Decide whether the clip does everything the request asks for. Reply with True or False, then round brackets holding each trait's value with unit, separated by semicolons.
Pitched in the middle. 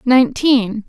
False (245 Hz)